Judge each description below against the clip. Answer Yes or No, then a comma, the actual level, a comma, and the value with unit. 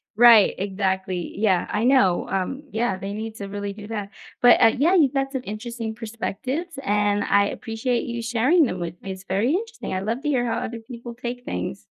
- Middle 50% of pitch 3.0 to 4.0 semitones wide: Yes, average, 3.7 semitones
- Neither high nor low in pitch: No, high, 225 Hz